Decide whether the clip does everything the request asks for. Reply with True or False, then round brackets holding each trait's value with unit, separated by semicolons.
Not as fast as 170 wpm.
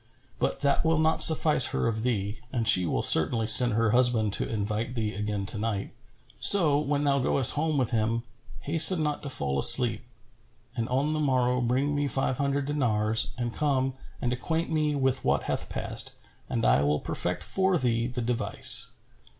False (180 wpm)